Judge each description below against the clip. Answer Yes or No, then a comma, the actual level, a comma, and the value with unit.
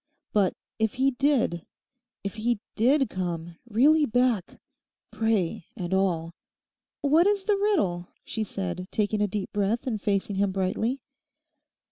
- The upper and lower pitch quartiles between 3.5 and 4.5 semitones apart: No, average, 5.3 semitones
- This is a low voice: No, high, 215 Hz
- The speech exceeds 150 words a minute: No, slow, 135 wpm